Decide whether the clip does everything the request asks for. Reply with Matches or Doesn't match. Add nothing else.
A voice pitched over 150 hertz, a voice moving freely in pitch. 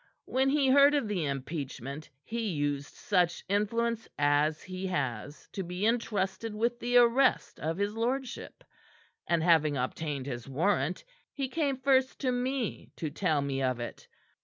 Matches